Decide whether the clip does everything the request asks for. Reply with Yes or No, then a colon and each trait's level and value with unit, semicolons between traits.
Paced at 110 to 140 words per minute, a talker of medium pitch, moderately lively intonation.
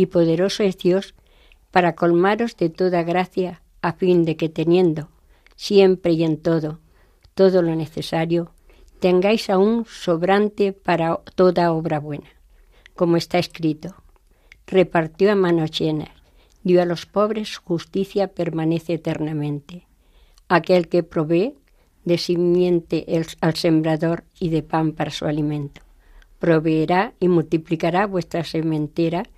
No: slow, 125 wpm; medium, 170 Hz; narrow, 2.3 semitones